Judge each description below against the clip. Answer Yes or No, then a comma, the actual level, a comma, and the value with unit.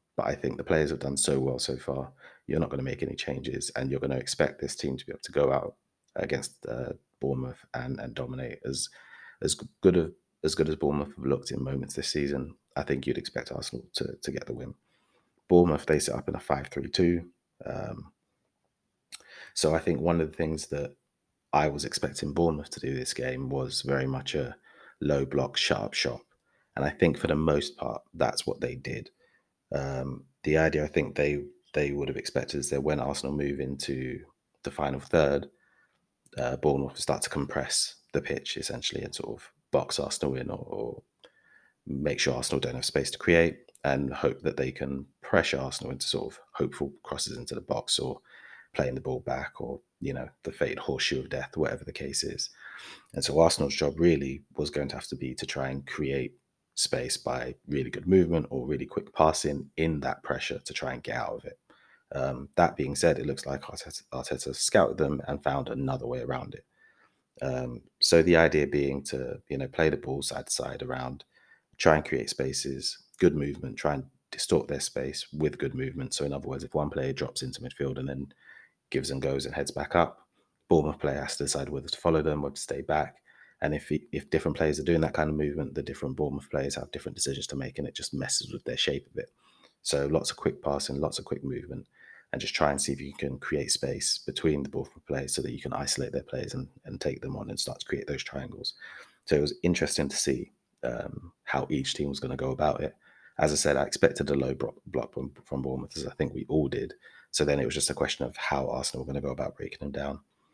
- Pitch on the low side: Yes, very low, 70 Hz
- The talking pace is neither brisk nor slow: No, fast, 225 wpm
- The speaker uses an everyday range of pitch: No, narrow, 1.9 semitones